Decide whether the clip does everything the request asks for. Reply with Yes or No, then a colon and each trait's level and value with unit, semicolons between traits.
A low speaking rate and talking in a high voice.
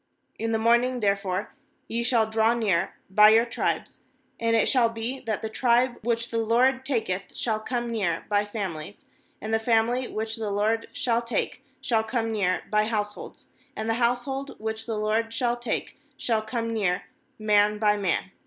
No: average, 175 wpm; high, 225 Hz